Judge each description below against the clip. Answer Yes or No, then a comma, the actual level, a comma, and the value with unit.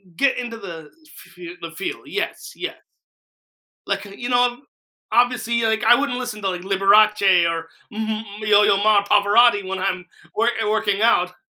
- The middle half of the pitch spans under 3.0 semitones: No, average, 3.4 semitones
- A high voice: Yes, high, 210 Hz